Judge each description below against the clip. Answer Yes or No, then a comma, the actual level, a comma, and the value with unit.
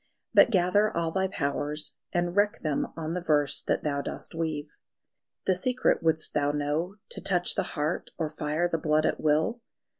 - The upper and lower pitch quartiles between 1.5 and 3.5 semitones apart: Yes, average, 3.2 semitones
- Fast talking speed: No, average, 180 wpm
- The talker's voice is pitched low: No, medium, 160 Hz